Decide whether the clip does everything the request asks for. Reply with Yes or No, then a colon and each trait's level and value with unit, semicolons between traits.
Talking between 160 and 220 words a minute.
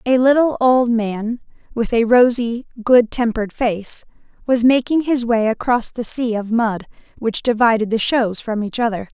Yes: average, 170 wpm